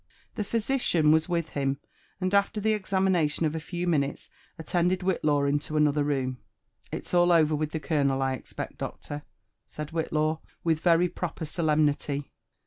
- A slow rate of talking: No, average, 160 wpm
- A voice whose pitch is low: No, medium, 155 Hz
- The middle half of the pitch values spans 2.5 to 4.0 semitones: Yes, average, 3.2 semitones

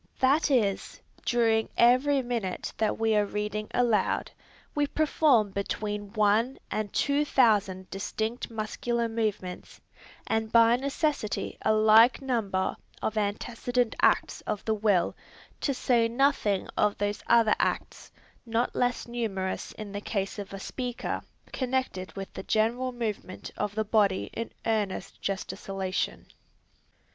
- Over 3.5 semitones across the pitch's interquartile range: No, average, 3.0 semitones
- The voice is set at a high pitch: Yes, high, 220 Hz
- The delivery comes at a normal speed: No, slow, 130 wpm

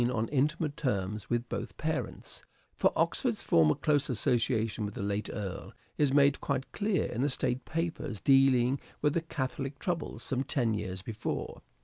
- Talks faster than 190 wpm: No, average, 160 wpm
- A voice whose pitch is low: Yes, low, 130 Hz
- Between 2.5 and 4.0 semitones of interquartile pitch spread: No, average, 5.0 semitones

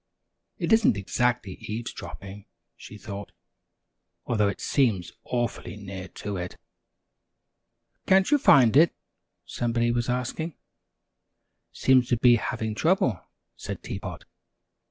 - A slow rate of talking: Yes, slow, 115 wpm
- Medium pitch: No, low, 120 Hz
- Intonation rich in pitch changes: No, average, 3.9 semitones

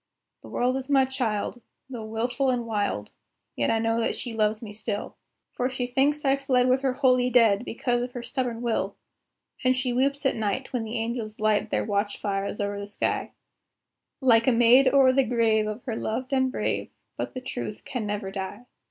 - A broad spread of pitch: No, average, 3.1 semitones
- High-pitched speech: Yes, high, 240 Hz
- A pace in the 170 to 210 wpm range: Yes, average, 200 wpm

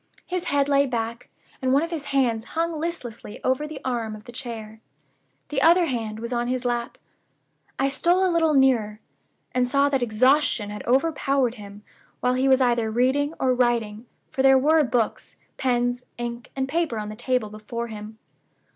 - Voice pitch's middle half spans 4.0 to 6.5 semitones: No, average, 3.3 semitones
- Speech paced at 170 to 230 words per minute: Yes, average, 180 wpm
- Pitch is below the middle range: No, very high, 250 Hz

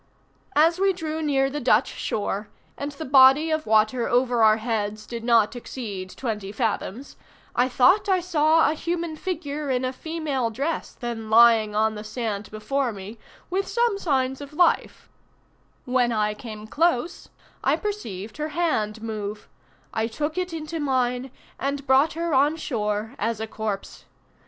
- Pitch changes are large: Yes, wide, 5.9 semitones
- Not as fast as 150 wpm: No, average, 160 wpm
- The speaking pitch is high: Yes, very high, 255 Hz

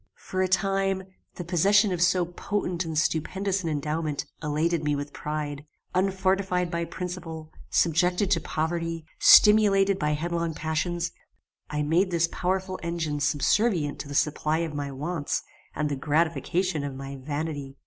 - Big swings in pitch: No, average, 3.6 semitones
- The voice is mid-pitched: Yes, medium, 165 Hz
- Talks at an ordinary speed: Yes, average, 150 wpm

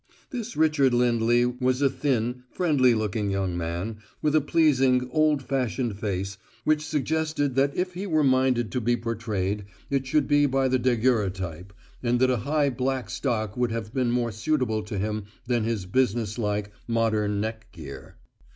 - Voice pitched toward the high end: No, low, 120 Hz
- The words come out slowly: No, average, 165 wpm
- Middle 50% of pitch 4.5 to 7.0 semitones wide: No, average, 4.1 semitones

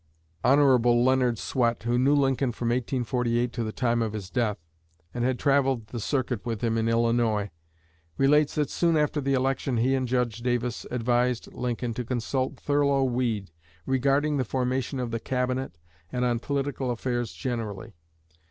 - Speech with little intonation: Yes, narrow, 2.2 semitones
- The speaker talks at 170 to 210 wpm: No, average, 160 wpm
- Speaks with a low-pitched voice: Yes, low, 125 Hz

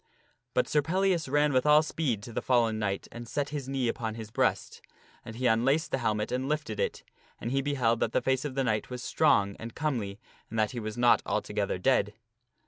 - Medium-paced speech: No, fast, 220 wpm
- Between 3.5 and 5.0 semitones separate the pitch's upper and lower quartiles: Yes, average, 4.2 semitones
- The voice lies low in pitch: Yes, low, 125 Hz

